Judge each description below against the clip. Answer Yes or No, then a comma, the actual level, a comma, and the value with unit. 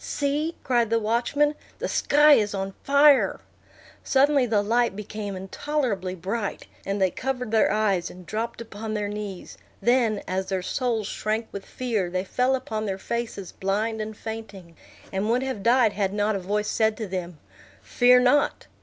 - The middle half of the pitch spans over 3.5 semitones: Yes, average, 3.9 semitones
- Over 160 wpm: Yes, average, 170 wpm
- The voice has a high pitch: Yes, high, 215 Hz